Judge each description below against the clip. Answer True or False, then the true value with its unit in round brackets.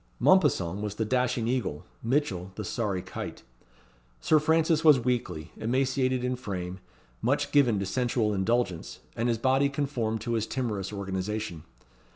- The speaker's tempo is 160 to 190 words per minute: False (145 wpm)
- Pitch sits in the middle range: False (115 Hz)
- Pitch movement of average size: True (4.9 semitones)